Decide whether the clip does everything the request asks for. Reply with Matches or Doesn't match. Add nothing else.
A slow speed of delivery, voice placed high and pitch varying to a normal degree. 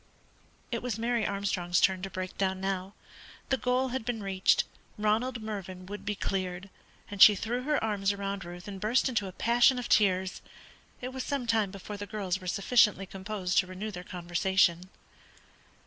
Doesn't match